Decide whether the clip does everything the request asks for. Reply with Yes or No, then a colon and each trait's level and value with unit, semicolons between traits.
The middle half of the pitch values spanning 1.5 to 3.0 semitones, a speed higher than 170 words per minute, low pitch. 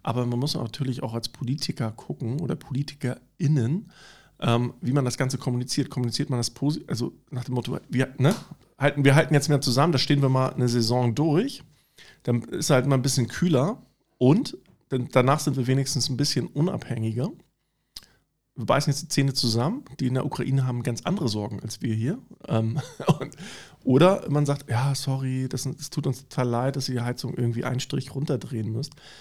Yes: average, 2.7 semitones; fast, 190 wpm; low, 130 Hz